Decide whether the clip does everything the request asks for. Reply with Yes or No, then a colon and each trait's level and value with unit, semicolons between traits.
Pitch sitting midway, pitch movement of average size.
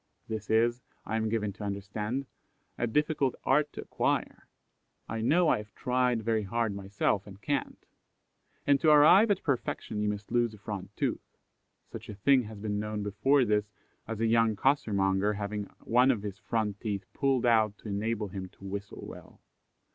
No: low, 110 Hz; average, 3.3 semitones